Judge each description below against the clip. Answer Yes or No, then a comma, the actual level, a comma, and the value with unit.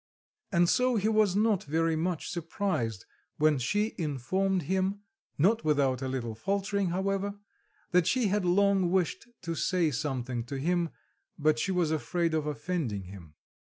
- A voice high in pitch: No, medium, 170 Hz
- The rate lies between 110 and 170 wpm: Yes, average, 155 wpm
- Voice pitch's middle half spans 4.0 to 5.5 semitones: Yes, average, 5.1 semitones